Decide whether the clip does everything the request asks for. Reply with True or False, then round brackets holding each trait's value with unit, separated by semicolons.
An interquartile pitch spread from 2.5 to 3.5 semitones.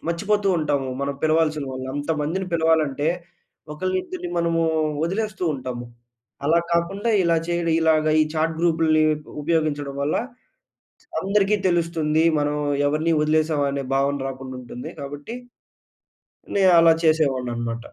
True (3.0 semitones)